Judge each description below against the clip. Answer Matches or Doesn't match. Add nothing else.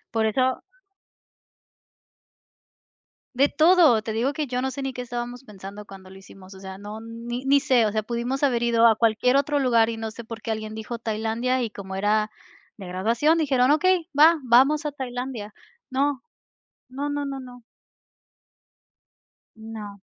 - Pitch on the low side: Doesn't match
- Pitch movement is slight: Doesn't match